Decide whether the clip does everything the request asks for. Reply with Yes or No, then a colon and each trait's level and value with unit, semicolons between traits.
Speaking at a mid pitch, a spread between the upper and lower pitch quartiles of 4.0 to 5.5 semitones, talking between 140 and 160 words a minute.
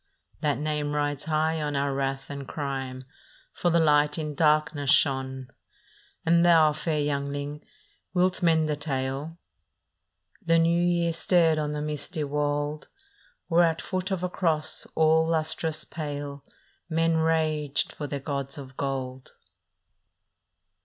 No: medium, 150 Hz; narrow, 2.4 semitones; average, 145 wpm